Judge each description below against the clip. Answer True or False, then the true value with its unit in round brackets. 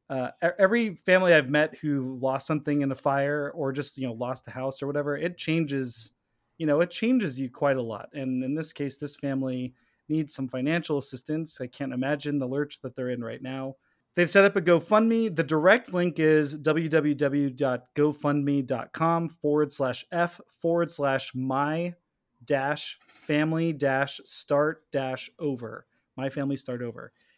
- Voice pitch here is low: False (145 Hz)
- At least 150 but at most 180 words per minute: True (160 wpm)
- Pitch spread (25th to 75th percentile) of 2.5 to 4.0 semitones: True (3.3 semitones)